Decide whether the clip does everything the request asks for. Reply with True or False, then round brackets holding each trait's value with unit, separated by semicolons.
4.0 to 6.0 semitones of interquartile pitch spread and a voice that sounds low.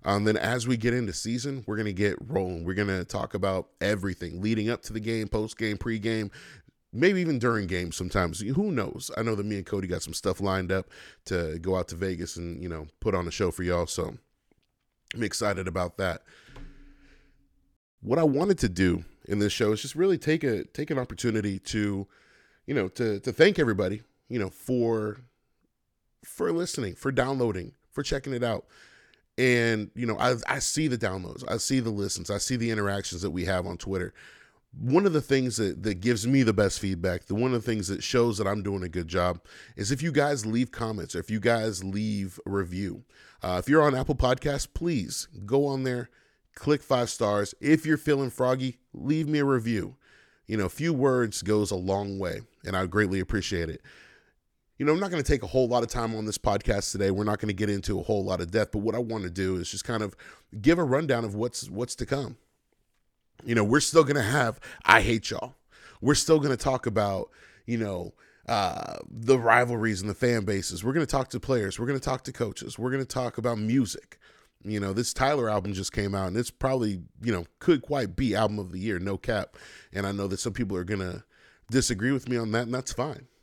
True (4.7 semitones; 110 Hz)